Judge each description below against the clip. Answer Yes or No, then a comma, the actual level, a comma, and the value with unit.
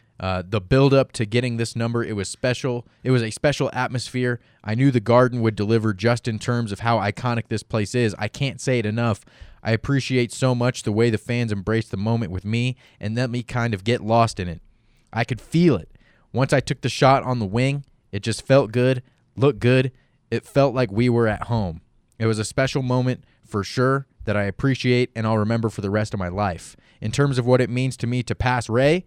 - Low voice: Yes, low, 120 Hz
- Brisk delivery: Yes, fast, 230 wpm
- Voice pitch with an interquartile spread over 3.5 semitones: No, narrow, 2.6 semitones